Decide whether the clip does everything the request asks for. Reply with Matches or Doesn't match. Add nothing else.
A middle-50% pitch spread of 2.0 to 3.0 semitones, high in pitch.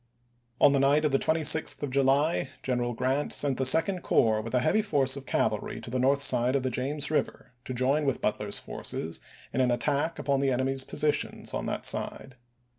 Doesn't match